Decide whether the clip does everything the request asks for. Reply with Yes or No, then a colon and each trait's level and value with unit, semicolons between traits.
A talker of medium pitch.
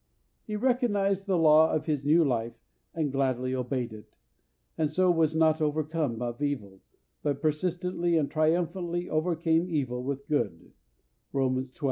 Yes: medium, 155 Hz